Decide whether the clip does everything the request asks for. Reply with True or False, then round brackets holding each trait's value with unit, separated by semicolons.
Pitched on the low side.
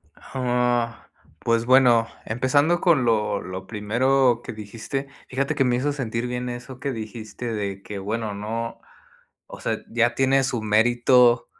True (120 Hz)